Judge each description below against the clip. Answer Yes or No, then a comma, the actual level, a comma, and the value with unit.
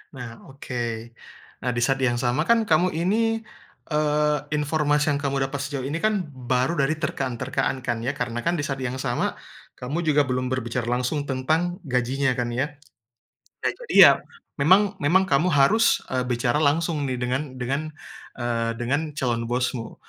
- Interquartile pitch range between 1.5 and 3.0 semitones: No, average, 3.6 semitones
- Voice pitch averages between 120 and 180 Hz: Yes, medium, 140 Hz